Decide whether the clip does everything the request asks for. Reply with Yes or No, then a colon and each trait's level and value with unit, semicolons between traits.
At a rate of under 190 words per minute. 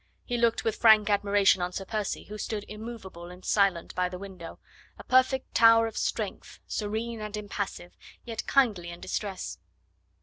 Yes: average, 165 wpm